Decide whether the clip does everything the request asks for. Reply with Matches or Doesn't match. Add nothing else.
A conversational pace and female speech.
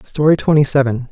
Doesn't match